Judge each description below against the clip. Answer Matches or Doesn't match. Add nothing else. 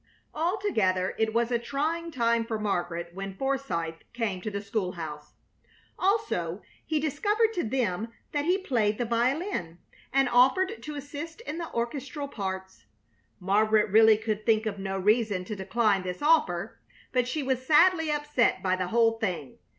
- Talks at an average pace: Matches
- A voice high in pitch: Matches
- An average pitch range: Doesn't match